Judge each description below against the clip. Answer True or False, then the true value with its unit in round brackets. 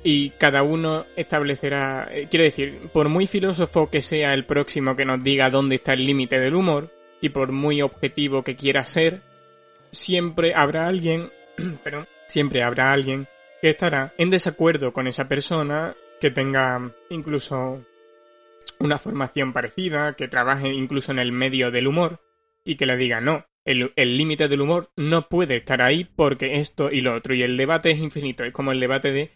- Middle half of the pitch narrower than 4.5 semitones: True (3.0 semitones)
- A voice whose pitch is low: False (145 Hz)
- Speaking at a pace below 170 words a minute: False (175 wpm)